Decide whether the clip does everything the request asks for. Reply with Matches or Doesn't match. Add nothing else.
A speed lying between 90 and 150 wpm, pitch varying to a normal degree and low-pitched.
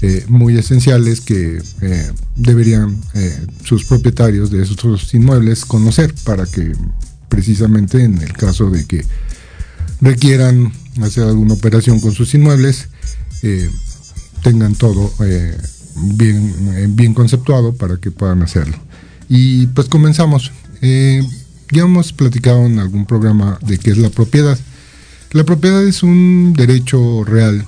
Matches